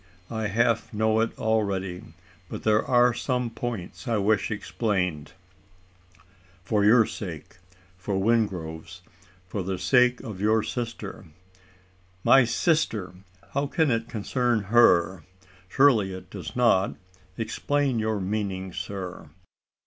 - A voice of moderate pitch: No, low, 110 Hz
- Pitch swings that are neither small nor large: Yes, average, 4.0 semitones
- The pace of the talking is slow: Yes, slow, 120 wpm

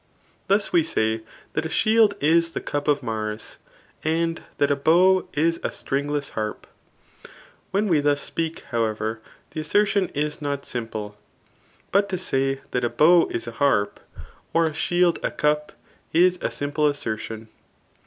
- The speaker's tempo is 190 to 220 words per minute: No, average, 155 wpm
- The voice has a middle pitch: Yes, medium, 150 Hz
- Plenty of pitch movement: Yes, wide, 5.7 semitones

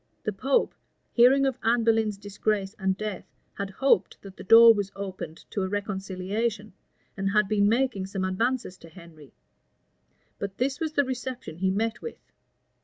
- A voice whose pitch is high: Yes, high, 205 Hz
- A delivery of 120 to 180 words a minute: Yes, average, 170 wpm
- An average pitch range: Yes, average, 3.5 semitones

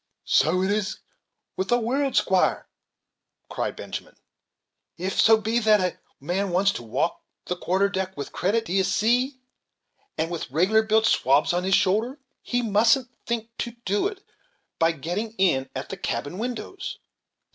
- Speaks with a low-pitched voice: No, high, 200 Hz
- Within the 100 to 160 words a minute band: Yes, average, 155 wpm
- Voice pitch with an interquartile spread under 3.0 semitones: No, average, 4.2 semitones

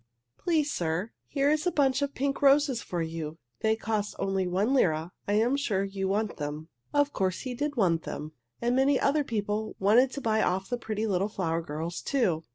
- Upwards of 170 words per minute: Yes, average, 200 wpm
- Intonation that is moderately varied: No, wide, 7.0 semitones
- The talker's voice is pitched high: Yes, high, 215 Hz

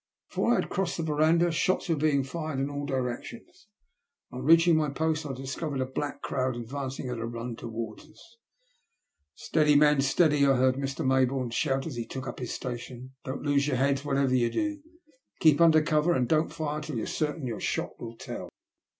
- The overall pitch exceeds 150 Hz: No, medium, 140 Hz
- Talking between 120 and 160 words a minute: No, fast, 205 wpm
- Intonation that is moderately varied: Yes, average, 3.3 semitones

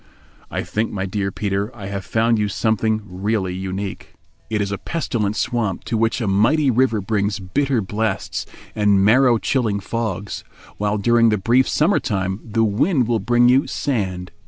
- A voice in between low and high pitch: No, low, 110 Hz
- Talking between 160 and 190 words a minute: Yes, average, 170 wpm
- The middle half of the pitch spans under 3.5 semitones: Yes, average, 3.0 semitones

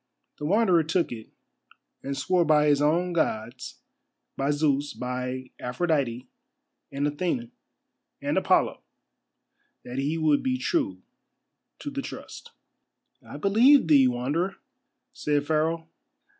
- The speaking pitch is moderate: Yes, medium, 150 Hz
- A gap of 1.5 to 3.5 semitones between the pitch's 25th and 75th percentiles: No, average, 4.8 semitones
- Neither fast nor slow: No, slow, 115 wpm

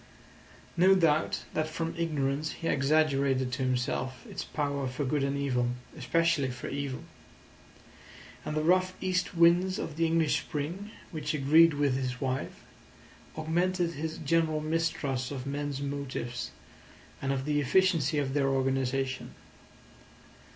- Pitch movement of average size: Yes, average, 3.5 semitones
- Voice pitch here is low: No, medium, 145 Hz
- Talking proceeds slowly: Yes, slow, 130 wpm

